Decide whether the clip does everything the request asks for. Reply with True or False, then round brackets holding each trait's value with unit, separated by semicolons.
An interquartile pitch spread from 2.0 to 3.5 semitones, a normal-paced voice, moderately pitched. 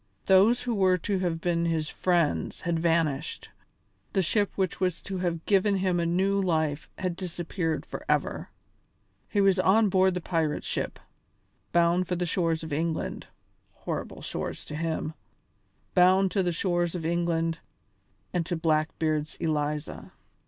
True (2.4 semitones; 150 wpm; 175 Hz)